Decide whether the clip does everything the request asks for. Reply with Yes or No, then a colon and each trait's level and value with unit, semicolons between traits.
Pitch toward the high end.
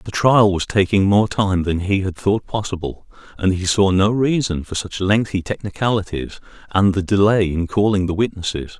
No: very low, 95 Hz